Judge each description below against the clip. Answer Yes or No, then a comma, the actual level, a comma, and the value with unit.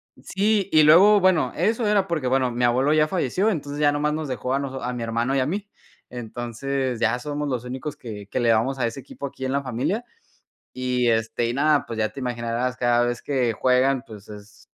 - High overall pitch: No, low, 130 Hz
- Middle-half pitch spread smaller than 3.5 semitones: No, average, 3.8 semitones